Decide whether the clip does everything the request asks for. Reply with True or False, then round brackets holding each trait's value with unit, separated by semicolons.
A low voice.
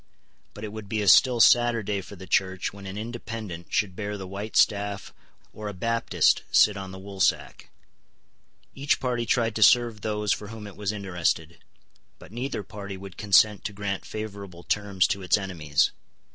True (100 Hz)